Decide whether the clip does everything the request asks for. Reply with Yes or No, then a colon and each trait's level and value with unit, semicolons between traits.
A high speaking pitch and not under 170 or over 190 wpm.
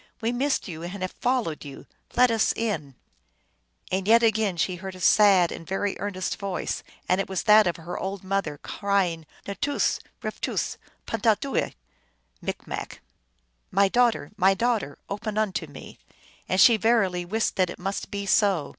Yes: high, 195 Hz; average, 180 wpm